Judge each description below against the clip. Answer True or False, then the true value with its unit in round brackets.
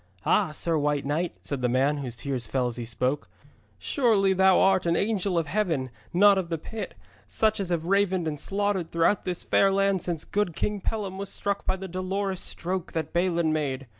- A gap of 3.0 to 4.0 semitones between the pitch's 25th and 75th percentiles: False (4.7 semitones)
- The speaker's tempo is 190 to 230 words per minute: True (200 wpm)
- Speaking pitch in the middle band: True (180 Hz)